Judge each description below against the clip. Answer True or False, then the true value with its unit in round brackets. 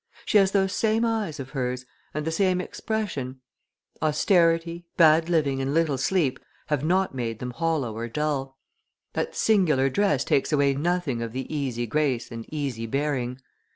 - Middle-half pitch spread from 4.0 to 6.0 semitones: True (4.8 semitones)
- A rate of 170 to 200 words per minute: False (160 wpm)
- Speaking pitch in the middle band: True (150 Hz)